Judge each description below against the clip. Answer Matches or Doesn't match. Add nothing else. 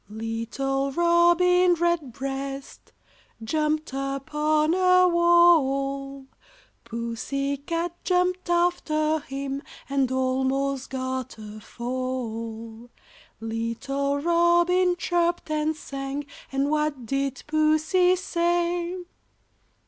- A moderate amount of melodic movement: Matches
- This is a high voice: Matches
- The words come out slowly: Matches